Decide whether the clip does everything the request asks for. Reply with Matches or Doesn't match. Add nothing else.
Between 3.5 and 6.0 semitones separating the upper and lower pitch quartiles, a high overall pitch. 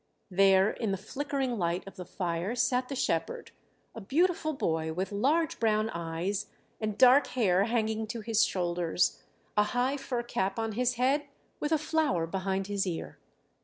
Matches